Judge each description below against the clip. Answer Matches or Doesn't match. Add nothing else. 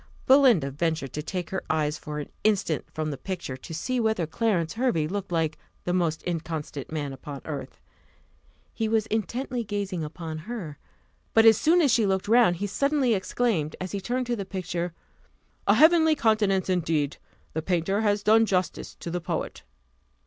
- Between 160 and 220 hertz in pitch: Matches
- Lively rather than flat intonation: Matches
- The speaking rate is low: Doesn't match